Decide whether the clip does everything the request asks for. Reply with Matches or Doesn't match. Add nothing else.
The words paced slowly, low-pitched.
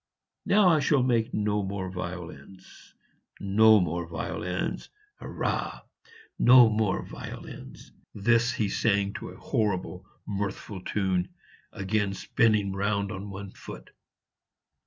Matches